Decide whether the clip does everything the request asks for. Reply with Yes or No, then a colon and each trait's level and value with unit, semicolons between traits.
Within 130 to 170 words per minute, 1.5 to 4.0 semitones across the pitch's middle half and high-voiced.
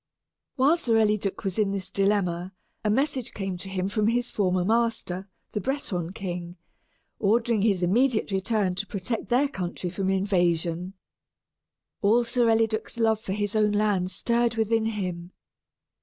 Yes: average, 150 wpm; average, 3.4 semitones; high, 205 Hz